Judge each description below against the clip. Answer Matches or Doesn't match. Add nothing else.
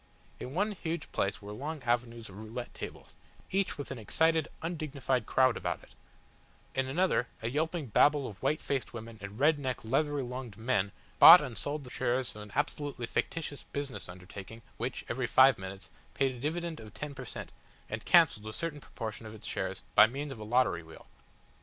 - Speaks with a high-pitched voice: Doesn't match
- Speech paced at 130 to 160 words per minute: Doesn't match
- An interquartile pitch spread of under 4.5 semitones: Doesn't match